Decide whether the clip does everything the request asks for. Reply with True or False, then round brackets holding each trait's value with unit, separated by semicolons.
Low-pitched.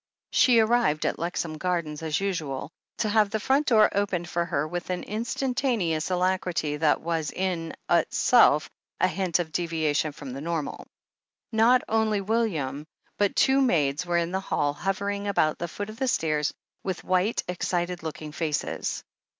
False (175 Hz)